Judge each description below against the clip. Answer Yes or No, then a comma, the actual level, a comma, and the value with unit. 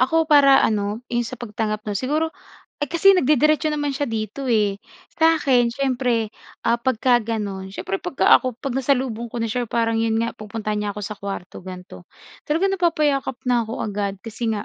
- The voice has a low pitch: No, high, 235 Hz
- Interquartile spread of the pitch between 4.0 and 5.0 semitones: Yes, average, 4.5 semitones